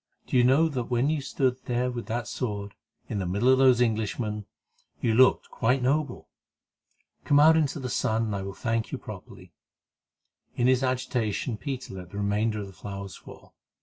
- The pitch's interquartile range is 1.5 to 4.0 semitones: Yes, average, 3.7 semitones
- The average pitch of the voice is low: Yes, low, 120 Hz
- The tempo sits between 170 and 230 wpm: Yes, average, 185 wpm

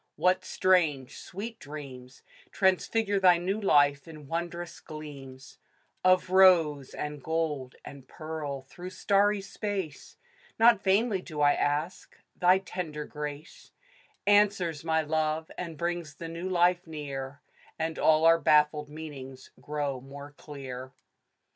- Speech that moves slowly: Yes, slow, 125 wpm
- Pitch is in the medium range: Yes, medium, 160 Hz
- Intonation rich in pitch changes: No, average, 4.0 semitones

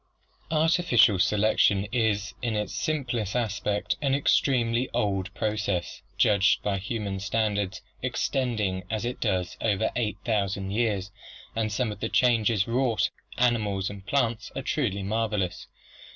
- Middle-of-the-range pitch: No, low, 110 Hz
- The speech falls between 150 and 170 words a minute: No, slow, 135 wpm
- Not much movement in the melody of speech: No, average, 3.0 semitones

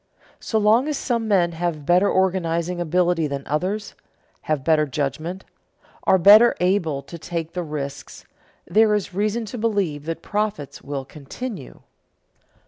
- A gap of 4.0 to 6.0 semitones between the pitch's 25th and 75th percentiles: Yes, average, 5.1 semitones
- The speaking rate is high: No, average, 140 wpm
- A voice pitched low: No, medium, 175 Hz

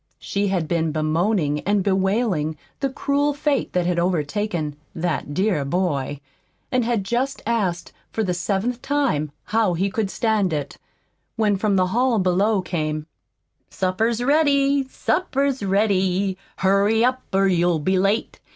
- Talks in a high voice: Yes, high, 195 Hz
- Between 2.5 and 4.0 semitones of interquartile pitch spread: No, average, 4.9 semitones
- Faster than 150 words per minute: No, average, 140 wpm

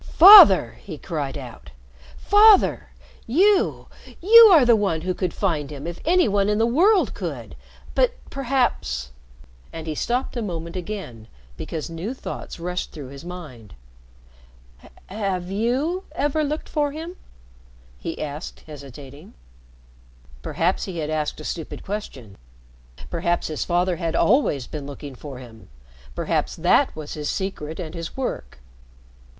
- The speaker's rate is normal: Yes, average, 145 wpm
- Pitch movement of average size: No, wide, 8.6 semitones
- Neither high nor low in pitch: Yes, medium, 175 Hz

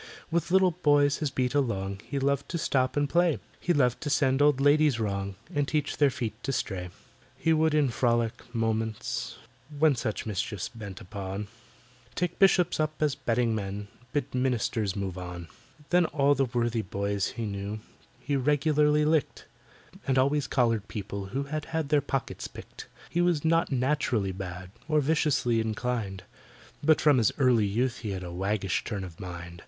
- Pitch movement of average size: No, wide, 6.3 semitones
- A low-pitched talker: Yes, low, 125 Hz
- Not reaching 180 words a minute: Yes, average, 170 wpm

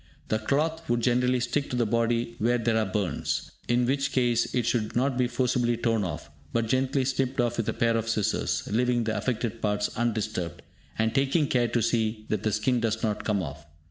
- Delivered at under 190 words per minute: No, fast, 205 wpm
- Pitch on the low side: Yes, low, 115 Hz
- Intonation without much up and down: Yes, narrow, 2.3 semitones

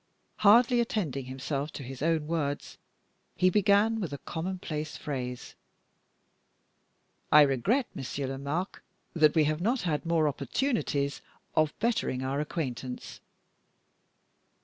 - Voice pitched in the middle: Yes, medium, 155 Hz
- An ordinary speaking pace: No, slow, 115 wpm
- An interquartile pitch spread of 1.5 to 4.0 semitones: No, average, 5.2 semitones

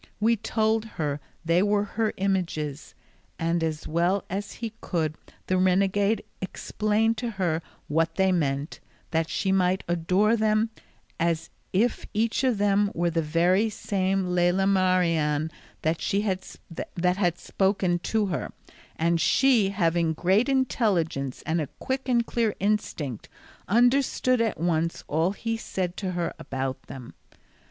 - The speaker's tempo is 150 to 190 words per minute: No, slow, 135 wpm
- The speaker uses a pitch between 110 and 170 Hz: No, medium, 185 Hz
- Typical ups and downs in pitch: Yes, average, 4.2 semitones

